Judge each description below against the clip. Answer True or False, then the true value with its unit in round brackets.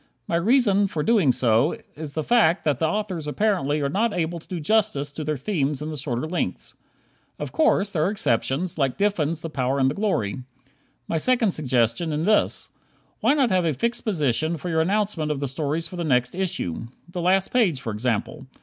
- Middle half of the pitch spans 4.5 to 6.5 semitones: True (5.6 semitones)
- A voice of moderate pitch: True (160 Hz)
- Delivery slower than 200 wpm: False (205 wpm)